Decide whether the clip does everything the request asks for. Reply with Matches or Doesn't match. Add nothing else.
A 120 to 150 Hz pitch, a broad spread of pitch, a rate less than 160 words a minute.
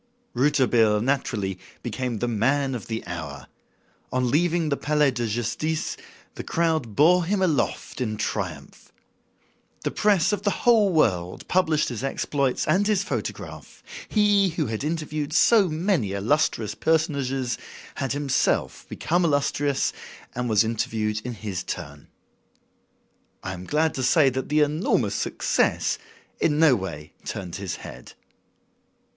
Matches